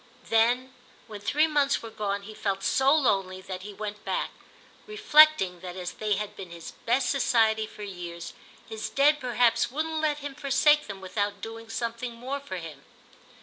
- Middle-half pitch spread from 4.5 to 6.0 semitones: Yes, wide, 5.6 semitones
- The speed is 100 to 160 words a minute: No, average, 175 wpm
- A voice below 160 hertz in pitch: No, high, 225 Hz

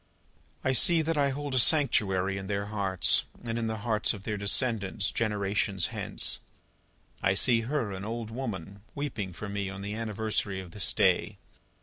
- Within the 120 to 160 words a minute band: No, average, 175 wpm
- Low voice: Yes, low, 105 Hz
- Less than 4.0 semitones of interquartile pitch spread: Yes, average, 3.3 semitones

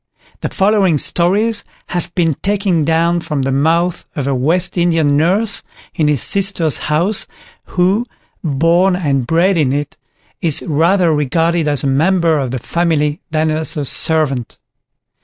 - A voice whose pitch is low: No, medium, 165 Hz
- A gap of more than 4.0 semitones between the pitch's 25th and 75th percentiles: No, average, 3.4 semitones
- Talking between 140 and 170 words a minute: Yes, average, 150 wpm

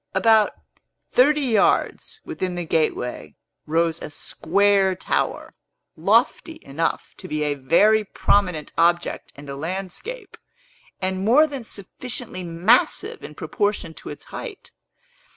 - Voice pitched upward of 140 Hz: Yes, high, 190 Hz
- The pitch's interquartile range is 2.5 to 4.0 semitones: No, wide, 5.5 semitones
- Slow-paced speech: Yes, slow, 120 wpm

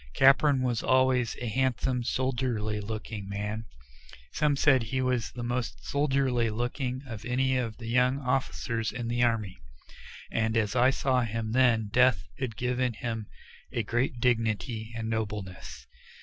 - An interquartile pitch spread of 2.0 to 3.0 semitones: Yes, narrow, 2.5 semitones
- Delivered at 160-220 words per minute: No, average, 150 wpm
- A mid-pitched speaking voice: No, low, 120 Hz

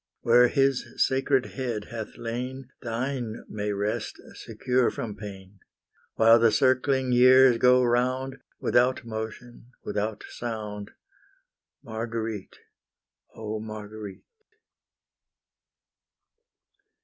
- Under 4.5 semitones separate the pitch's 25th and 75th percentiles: Yes, average, 2.9 semitones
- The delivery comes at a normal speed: No, slow, 90 wpm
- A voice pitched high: No, low, 120 Hz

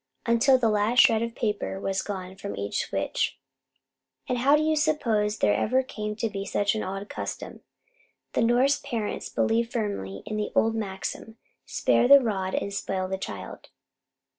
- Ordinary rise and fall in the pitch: Yes, average, 3.5 semitones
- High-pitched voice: Yes, high, 215 Hz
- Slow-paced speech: No, average, 170 wpm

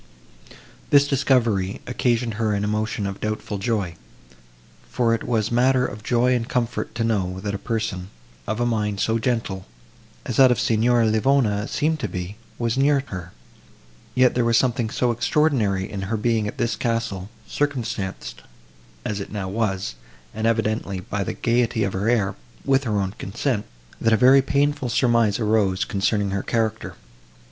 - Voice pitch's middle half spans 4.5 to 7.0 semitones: No, average, 3.2 semitones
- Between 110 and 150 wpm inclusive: No, average, 165 wpm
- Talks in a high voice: No, low, 110 Hz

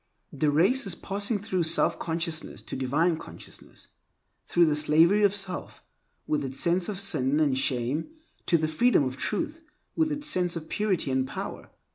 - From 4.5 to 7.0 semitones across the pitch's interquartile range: Yes, average, 5.1 semitones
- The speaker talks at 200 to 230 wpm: No, average, 170 wpm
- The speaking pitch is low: No, medium, 170 Hz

